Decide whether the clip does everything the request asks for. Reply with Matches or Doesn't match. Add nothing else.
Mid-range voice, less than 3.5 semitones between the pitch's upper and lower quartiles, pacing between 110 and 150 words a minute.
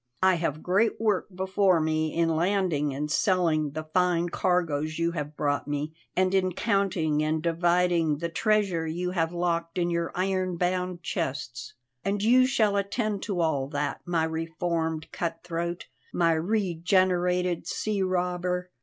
Matches